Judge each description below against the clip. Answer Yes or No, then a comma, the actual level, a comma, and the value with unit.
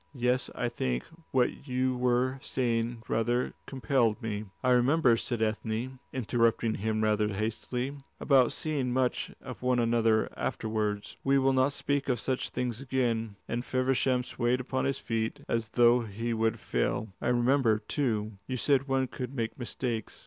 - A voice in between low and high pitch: No, low, 120 Hz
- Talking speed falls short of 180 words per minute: Yes, average, 155 wpm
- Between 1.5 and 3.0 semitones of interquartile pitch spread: Yes, narrow, 2.6 semitones